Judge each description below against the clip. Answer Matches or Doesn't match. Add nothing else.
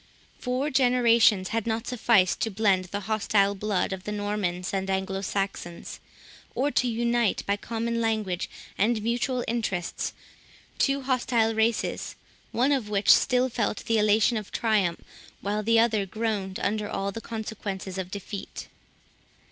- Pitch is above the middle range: Matches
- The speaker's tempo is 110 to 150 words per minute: Matches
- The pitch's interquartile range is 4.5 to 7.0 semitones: Doesn't match